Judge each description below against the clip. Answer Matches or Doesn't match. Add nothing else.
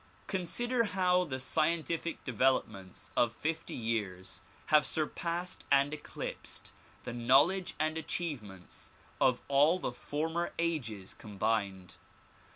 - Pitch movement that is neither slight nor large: Doesn't match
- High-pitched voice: Doesn't match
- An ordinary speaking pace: Doesn't match